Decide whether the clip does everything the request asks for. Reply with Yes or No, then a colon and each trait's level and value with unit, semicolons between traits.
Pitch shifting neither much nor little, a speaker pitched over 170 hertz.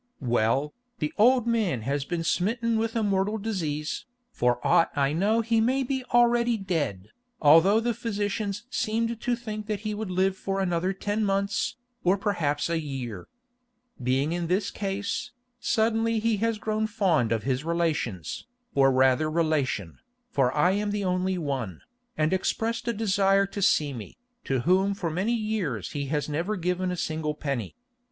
No: wide, 6.3 semitones; high, 190 Hz